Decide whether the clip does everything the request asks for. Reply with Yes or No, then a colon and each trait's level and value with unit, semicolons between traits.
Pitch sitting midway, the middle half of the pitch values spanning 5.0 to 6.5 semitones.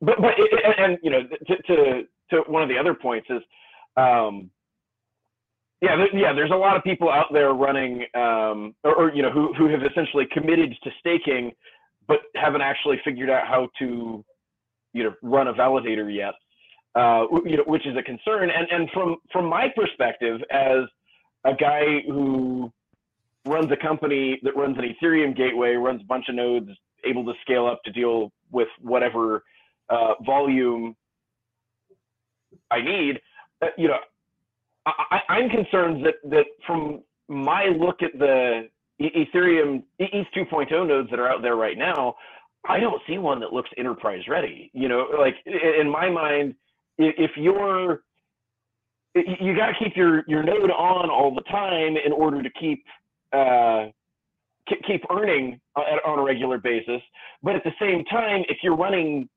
Yes: medium, 145 Hz; wide, 5.6 semitones